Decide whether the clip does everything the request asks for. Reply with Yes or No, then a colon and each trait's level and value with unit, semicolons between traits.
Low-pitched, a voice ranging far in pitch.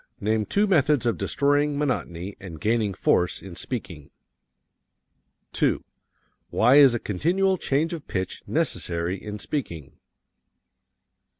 Yes: low, 115 Hz; wide, 7.8 semitones